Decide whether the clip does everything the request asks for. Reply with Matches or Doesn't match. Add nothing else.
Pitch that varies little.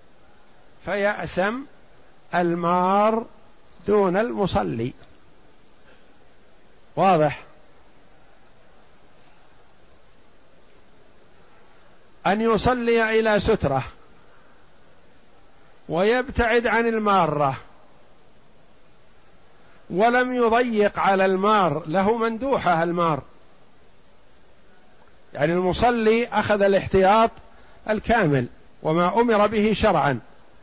Doesn't match